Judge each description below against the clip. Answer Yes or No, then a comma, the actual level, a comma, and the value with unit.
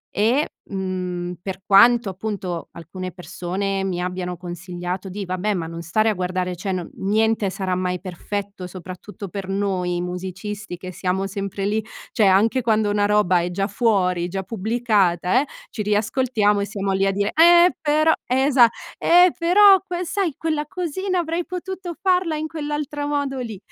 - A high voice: Yes, high, 200 Hz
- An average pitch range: No, wide, 5.9 semitones